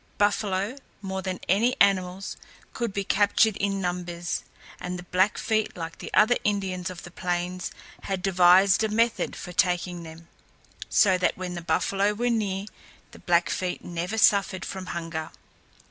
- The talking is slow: No, average, 155 wpm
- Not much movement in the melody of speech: Yes, narrow, 2.3 semitones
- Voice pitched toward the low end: No, medium, 185 Hz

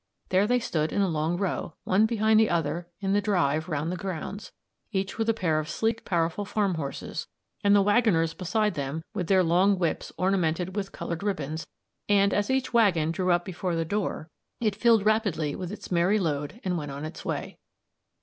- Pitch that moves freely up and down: No, average, 4.0 semitones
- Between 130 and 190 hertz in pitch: Yes, medium, 185 Hz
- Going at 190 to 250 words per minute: Yes, average, 200 wpm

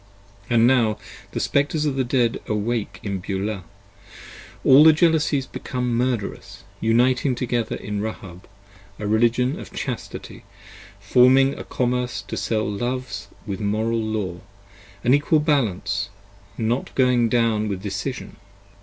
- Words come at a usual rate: No, slow, 130 wpm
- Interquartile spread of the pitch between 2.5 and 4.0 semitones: Yes, average, 3.6 semitones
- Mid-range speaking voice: No, low, 115 Hz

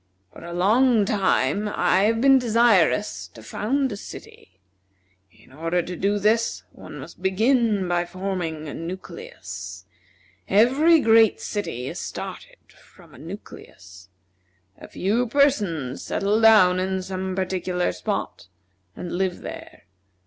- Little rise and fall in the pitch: No, average, 4.2 semitones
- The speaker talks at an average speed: No, slow, 130 wpm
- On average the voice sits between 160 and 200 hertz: Yes, high, 190 Hz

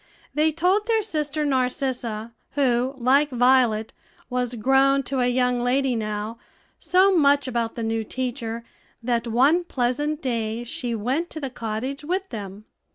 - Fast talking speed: No, average, 150 wpm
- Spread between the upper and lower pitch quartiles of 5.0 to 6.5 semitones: No, average, 3.7 semitones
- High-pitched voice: Yes, very high, 255 Hz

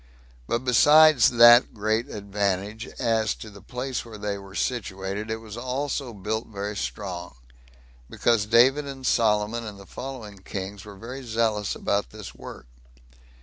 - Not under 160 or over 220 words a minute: No, average, 150 wpm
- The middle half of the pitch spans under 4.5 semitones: Yes, average, 2.8 semitones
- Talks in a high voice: No, low, 110 Hz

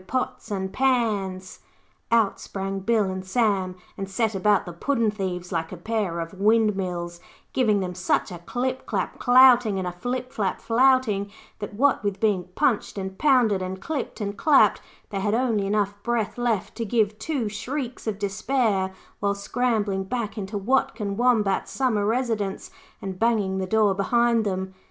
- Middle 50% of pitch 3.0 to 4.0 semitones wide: Yes, average, 3.7 semitones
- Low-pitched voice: No, high, 210 Hz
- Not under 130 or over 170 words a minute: Yes, average, 165 wpm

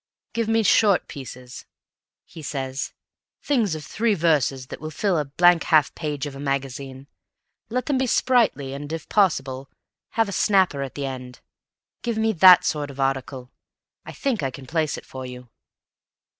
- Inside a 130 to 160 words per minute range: No, average, 170 wpm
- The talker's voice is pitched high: No, medium, 150 Hz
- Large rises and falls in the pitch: Yes, wide, 6.7 semitones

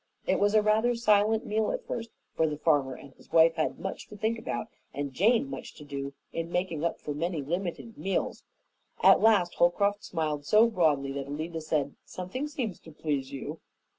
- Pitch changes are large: Yes, wide, 6.2 semitones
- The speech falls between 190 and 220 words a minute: Yes, average, 195 wpm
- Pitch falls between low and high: Yes, medium, 170 Hz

